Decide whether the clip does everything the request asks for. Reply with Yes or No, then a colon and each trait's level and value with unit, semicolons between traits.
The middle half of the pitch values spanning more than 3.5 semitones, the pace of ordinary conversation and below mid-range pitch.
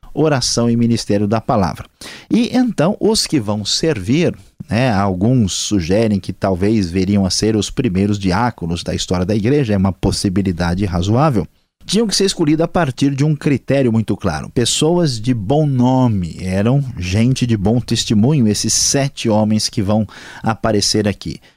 Yes: average, 5.3 semitones; average, 160 wpm; low, 110 Hz